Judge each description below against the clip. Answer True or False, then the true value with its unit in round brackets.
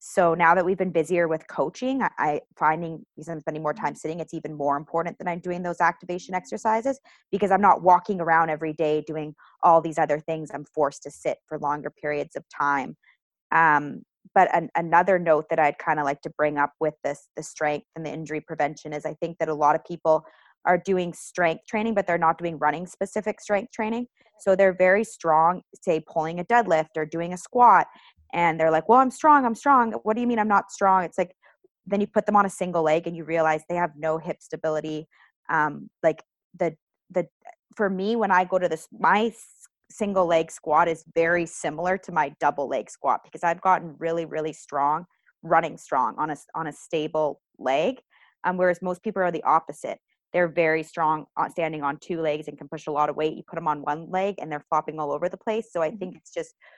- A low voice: False (165 Hz)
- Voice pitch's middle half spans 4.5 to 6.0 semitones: False (3.2 semitones)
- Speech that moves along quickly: True (230 wpm)